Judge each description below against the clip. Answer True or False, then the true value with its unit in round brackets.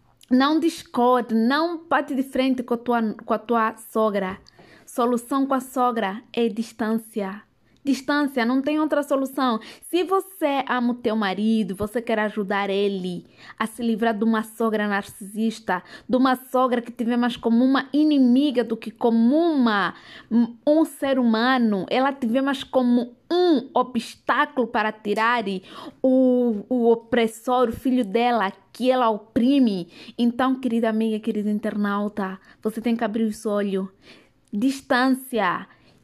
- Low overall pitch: False (235 Hz)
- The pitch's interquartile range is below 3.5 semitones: True (3.0 semitones)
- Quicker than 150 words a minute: False (145 wpm)